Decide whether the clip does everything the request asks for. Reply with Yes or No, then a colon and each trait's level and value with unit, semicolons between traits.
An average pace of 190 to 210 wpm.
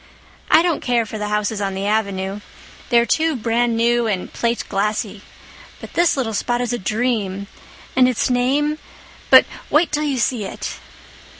No: average, 155 wpm